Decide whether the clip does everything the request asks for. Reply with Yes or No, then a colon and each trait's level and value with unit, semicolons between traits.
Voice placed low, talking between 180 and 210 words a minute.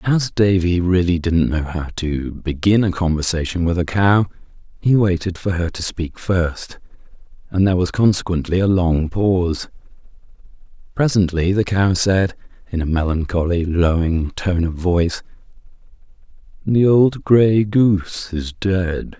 No: very low, 90 Hz; average, 140 wpm